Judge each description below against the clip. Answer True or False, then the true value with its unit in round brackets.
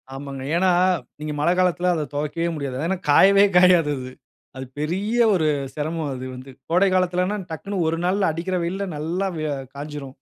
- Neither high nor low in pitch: True (165 Hz)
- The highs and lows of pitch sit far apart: False (3.8 semitones)